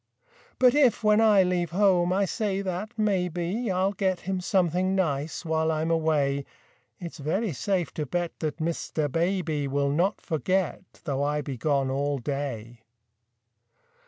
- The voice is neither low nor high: Yes, medium, 170 Hz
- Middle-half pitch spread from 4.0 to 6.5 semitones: Yes, average, 4.5 semitones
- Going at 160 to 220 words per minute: No, average, 150 wpm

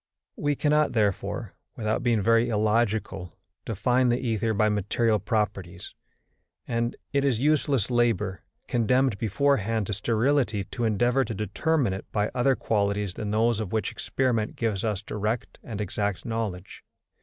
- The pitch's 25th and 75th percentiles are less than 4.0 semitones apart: Yes, average, 2.9 semitones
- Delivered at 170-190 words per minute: No, average, 145 wpm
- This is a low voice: Yes, low, 110 Hz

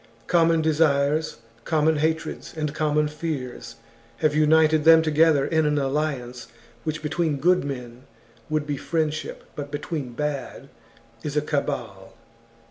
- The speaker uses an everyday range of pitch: No, narrow, 2.0 semitones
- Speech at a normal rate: No, slow, 125 wpm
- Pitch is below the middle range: No, medium, 150 Hz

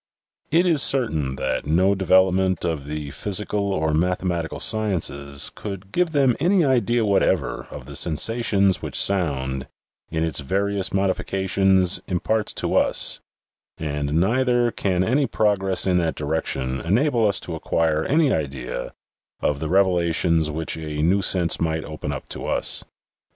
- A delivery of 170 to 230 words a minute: No, average, 145 wpm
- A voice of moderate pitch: No, very low, 90 Hz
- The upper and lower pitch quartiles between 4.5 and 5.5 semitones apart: Yes, average, 4.8 semitones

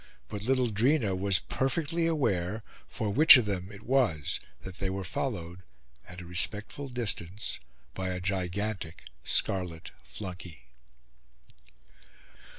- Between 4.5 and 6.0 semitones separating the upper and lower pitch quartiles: Yes, average, 5.2 semitones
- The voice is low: Yes, low, 100 Hz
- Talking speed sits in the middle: No, slow, 120 wpm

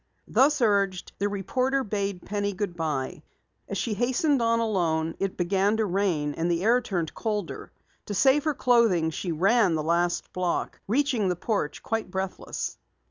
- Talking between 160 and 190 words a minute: Yes, average, 165 wpm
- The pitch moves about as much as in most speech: Yes, average, 4.8 semitones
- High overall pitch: Yes, high, 200 Hz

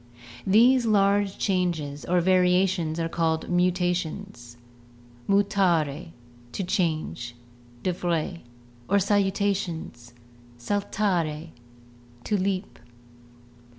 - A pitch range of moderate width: Yes, average, 3.5 semitones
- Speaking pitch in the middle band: Yes, medium, 180 Hz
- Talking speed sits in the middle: No, slow, 90 wpm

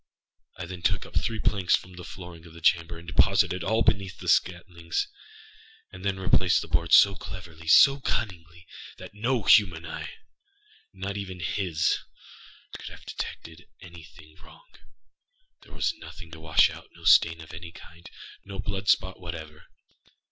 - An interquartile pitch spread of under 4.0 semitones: Yes, average, 2.9 semitones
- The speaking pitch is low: Yes, very low, 90 Hz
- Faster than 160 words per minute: No, average, 150 wpm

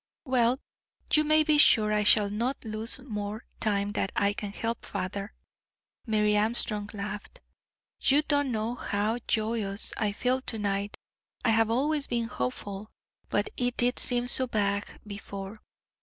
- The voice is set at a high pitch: Yes, high, 220 Hz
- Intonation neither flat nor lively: Yes, average, 3.2 semitones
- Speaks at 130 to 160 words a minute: Yes, average, 150 wpm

